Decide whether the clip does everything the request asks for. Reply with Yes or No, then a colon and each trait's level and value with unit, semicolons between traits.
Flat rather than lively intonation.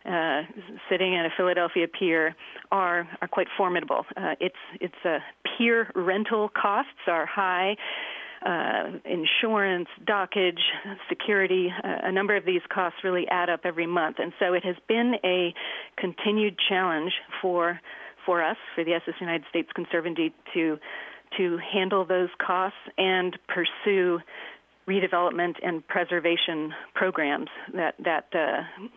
Yes: narrow, 2.1 semitones